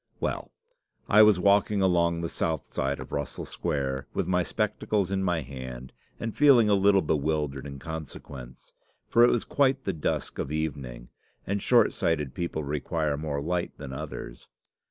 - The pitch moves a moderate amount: No, wide, 5.7 semitones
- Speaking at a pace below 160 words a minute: No, average, 170 wpm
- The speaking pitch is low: Yes, very low, 80 Hz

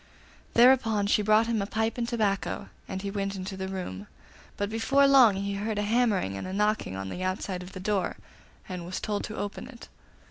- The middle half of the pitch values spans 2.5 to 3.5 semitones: Yes, average, 2.8 semitones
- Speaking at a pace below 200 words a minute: No, fast, 205 wpm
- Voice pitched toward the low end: No, high, 205 Hz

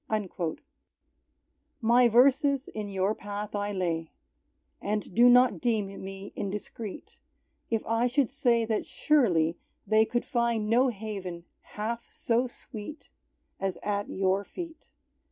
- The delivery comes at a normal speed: No, slow, 125 wpm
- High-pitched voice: Yes, high, 215 Hz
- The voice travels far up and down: No, average, 3.5 semitones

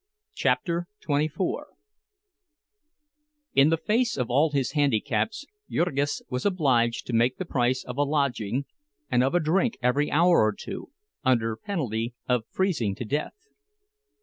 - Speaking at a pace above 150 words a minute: No, average, 140 wpm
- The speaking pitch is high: No, medium, 140 Hz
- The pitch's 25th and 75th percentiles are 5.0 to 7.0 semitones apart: Yes, wide, 5.5 semitones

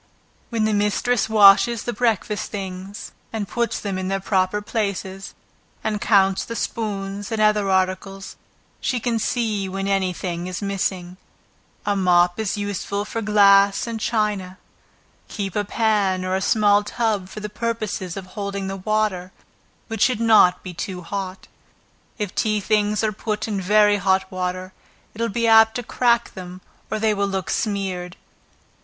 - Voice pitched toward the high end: Yes, high, 200 Hz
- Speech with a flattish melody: Yes, narrow, 2.3 semitones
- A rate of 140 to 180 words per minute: Yes, average, 160 wpm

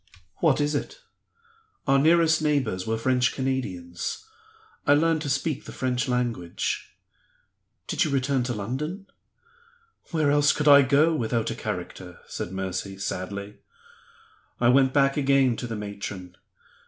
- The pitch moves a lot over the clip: Yes, wide, 5.9 semitones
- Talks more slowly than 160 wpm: Yes, average, 140 wpm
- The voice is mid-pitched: No, low, 130 Hz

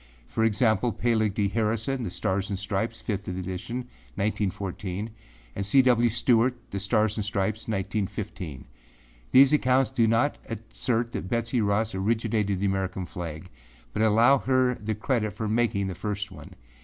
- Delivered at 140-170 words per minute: Yes, average, 155 wpm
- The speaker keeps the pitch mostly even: No, average, 3.1 semitones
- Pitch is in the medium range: No, low, 110 Hz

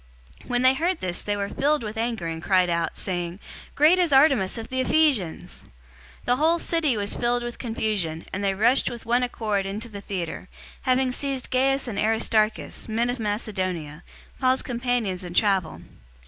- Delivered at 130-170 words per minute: No, average, 180 wpm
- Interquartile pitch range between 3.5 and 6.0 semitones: Yes, average, 5.0 semitones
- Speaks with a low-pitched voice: No, high, 225 Hz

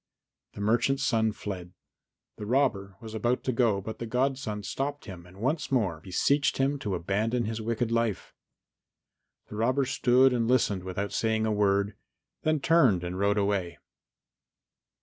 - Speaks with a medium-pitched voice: No, low, 110 Hz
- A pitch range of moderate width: Yes, average, 4.2 semitones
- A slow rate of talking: No, average, 155 wpm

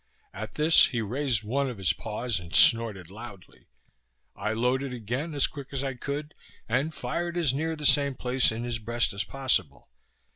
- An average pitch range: Yes, average, 4.2 semitones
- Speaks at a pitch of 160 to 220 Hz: No, low, 125 Hz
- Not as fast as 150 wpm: No, average, 180 wpm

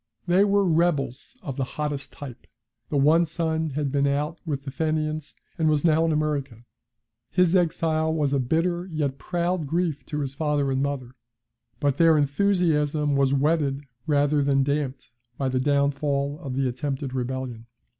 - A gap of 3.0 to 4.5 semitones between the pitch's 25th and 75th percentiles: No, narrow, 2.6 semitones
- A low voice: No, medium, 145 Hz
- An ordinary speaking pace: Yes, average, 165 wpm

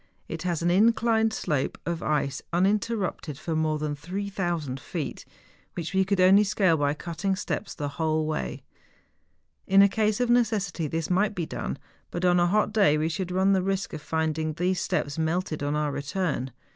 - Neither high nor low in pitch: Yes, medium, 175 Hz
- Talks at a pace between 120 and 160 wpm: No, average, 185 wpm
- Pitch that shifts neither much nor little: Yes, average, 4.1 semitones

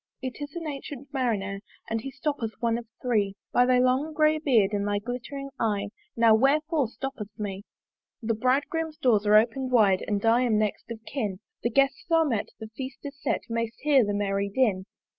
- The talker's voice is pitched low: No, high, 240 Hz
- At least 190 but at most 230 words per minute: Yes, average, 195 wpm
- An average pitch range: Yes, average, 4.5 semitones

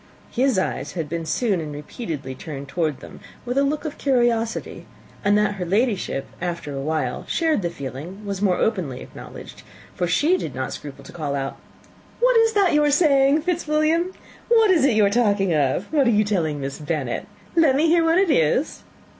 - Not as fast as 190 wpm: No, average, 195 wpm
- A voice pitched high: Yes, high, 205 Hz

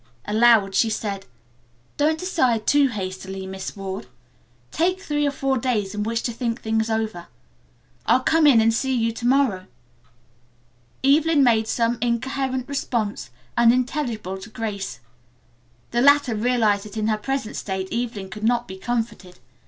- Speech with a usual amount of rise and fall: Yes, average, 3.9 semitones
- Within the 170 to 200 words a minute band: No, average, 150 wpm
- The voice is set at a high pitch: Yes, high, 230 Hz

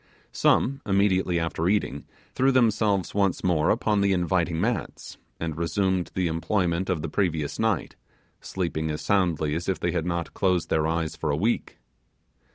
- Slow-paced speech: No, average, 165 wpm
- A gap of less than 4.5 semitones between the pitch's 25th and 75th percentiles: Yes, average, 3.4 semitones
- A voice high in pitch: No, very low, 90 Hz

